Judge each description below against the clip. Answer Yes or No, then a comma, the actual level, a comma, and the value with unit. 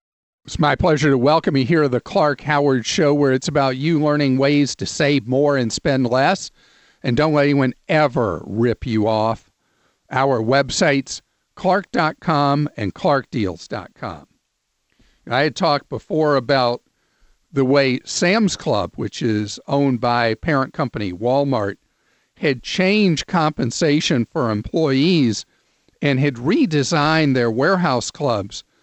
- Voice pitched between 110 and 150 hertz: Yes, medium, 140 Hz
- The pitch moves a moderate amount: Yes, average, 3.8 semitones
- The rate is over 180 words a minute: No, slow, 135 wpm